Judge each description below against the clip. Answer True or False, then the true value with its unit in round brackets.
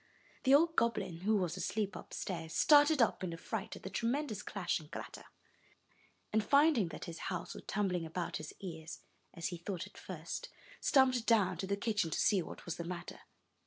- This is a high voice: True (195 Hz)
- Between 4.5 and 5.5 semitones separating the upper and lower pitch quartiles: True (5.2 semitones)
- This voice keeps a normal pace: True (195 wpm)